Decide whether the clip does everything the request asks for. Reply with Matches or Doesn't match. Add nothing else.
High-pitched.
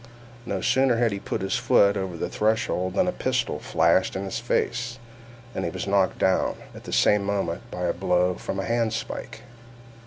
Doesn't match